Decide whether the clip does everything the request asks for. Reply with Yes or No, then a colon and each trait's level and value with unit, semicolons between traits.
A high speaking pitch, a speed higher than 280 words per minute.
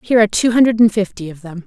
Yes: high, 210 Hz; fast, 290 wpm